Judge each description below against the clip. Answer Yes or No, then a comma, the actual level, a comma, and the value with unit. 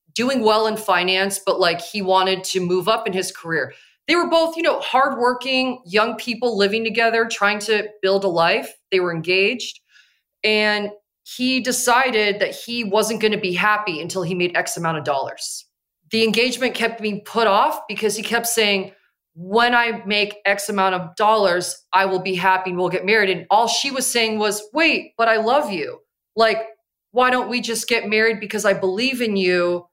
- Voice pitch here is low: No, high, 215 Hz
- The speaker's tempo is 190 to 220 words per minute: Yes, average, 195 wpm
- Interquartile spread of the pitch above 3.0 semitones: Yes, average, 3.7 semitones